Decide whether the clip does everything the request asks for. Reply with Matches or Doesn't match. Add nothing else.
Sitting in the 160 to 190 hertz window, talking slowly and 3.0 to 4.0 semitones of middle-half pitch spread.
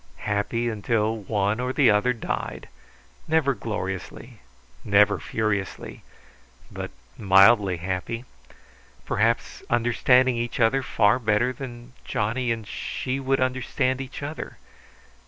Doesn't match